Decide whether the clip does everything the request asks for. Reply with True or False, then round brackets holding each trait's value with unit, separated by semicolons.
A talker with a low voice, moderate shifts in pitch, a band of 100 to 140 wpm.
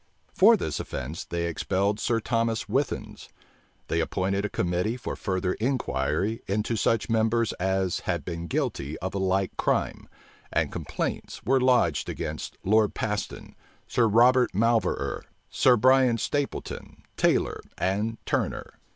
True (105 Hz; 3.9 semitones; 135 wpm)